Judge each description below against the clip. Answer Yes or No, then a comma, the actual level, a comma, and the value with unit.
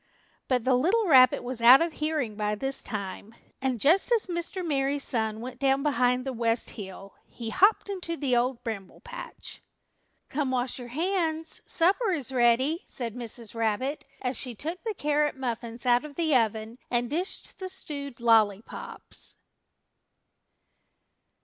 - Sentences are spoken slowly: No, average, 155 wpm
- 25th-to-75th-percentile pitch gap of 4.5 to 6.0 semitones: Yes, average, 5.2 semitones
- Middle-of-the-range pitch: No, very high, 260 Hz